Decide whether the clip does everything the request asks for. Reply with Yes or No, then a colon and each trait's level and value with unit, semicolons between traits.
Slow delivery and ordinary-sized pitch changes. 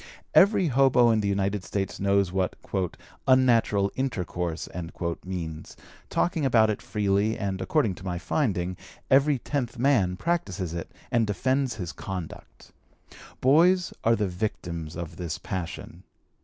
No: slow, 130 wpm; wide, 6.2 semitones